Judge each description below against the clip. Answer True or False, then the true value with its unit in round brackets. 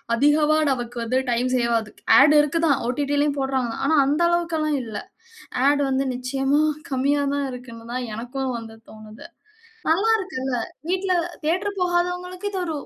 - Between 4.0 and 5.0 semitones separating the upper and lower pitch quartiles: True (4.6 semitones)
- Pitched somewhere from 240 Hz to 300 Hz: True (280 Hz)